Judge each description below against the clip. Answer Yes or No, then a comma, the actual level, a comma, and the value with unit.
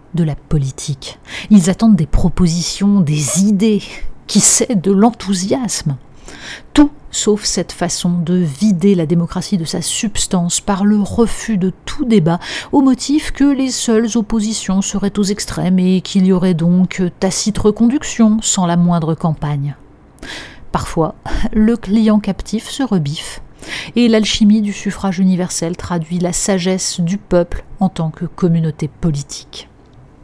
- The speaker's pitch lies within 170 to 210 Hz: Yes, high, 190 Hz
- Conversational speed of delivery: No, slow, 140 wpm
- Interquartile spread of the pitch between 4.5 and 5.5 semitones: No, average, 3.7 semitones